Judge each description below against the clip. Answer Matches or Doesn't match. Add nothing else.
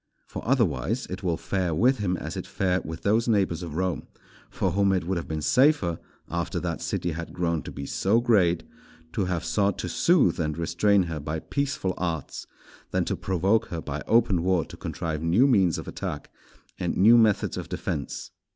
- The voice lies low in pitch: Matches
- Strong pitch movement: Doesn't match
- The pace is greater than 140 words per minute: Matches